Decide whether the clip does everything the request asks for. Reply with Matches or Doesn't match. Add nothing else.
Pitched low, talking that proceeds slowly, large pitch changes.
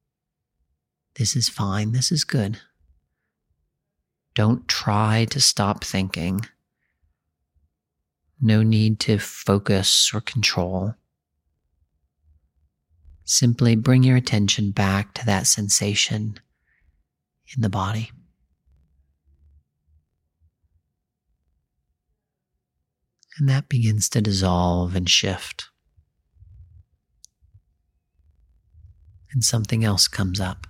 Matches